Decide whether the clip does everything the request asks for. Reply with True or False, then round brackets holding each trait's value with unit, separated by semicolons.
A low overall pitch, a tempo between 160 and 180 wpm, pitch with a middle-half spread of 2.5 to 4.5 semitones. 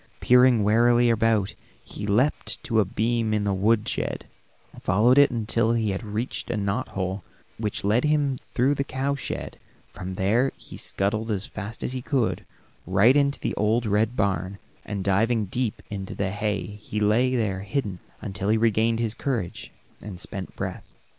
True (110 Hz; 175 wpm; 2.9 semitones)